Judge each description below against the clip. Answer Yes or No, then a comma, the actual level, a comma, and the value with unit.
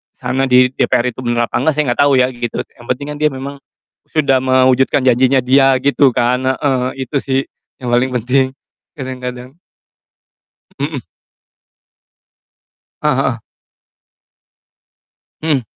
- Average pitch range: No, narrow, 1.6 semitones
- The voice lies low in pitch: Yes, low, 130 Hz